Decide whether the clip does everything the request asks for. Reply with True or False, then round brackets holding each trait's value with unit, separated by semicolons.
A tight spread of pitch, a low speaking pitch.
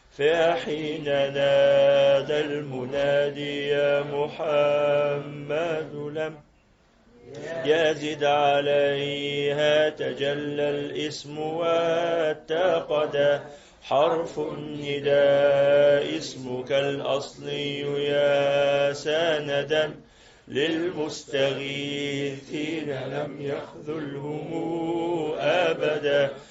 False (1.3 semitones; 145 Hz)